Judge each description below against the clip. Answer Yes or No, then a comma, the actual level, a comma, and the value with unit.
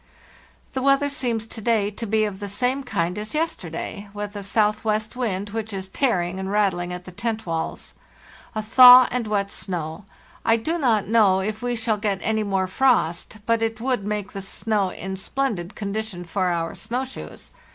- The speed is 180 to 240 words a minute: Yes, average, 185 wpm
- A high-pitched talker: Yes, high, 210 Hz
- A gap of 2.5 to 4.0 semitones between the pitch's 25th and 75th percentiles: Yes, average, 3.2 semitones